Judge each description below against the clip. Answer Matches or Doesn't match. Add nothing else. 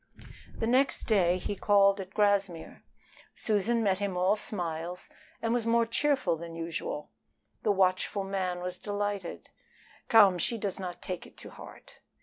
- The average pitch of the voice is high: Matches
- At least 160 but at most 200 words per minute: Doesn't match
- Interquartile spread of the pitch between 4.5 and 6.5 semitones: Doesn't match